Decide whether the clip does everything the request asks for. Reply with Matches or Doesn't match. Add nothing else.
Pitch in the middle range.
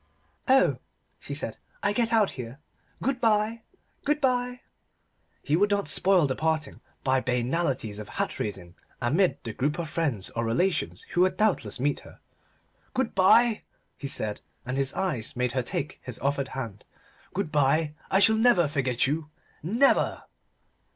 Matches